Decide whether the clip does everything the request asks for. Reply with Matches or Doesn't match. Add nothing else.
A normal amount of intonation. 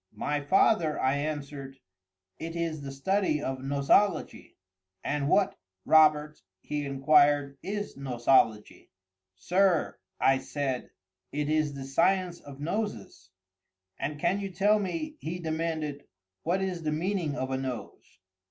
Matches